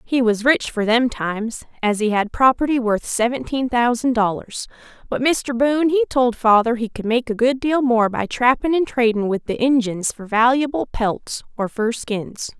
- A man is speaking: No, female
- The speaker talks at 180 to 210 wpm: Yes, average, 190 wpm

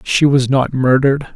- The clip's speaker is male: Yes, male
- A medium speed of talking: Yes, average, 175 wpm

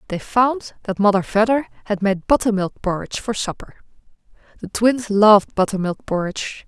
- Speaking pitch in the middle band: No, high, 210 Hz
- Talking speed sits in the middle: Yes, average, 145 wpm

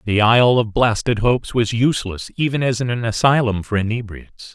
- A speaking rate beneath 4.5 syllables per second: No, 5.5 syllables/s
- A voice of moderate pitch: No, low, 115 Hz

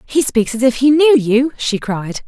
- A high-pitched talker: Yes, very high, 250 Hz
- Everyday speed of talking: No, fast, 235 wpm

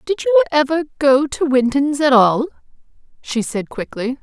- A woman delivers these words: Yes, female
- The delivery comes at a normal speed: Yes, average, 155 wpm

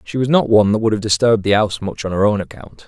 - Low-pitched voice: Yes, low, 105 Hz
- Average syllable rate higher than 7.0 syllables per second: Yes, 7.2 syllables/s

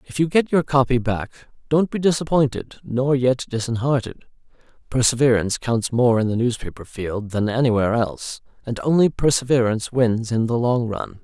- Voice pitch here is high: No, low, 125 Hz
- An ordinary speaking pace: Yes, average, 160 wpm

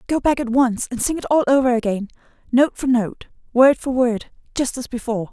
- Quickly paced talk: Yes, fast, 215 wpm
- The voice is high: Yes, very high, 250 Hz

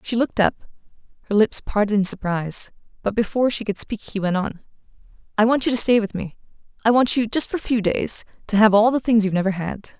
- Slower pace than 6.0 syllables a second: No, 6.3 syllables/s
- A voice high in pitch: Yes, high, 215 Hz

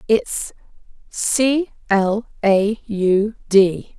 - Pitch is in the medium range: No, high, 210 Hz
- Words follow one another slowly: Yes, slow, 90 wpm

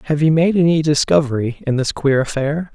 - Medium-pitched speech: Yes, medium, 150 Hz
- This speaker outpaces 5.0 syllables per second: Yes, 5.6 syllables/s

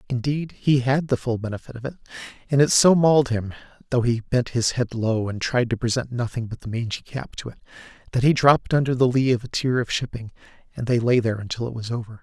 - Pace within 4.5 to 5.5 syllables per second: No, 6.1 syllables/s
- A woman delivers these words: No, male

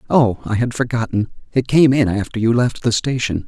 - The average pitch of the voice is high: No, low, 120 Hz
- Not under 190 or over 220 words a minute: Yes, fast, 205 wpm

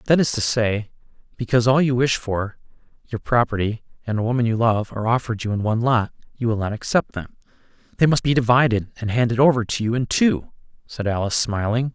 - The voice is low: Yes, low, 115 Hz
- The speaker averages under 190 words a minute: No, fast, 205 wpm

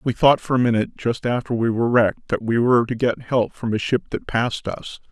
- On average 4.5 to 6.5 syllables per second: Yes, 6.0 syllables/s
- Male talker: Yes, male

